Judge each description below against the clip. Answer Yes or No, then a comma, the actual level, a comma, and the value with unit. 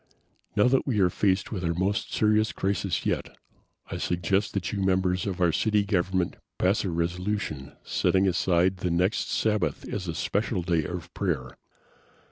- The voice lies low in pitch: Yes, very low, 95 Hz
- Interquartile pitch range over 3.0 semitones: No, average, 2.7 semitones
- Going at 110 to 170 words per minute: Yes, average, 165 wpm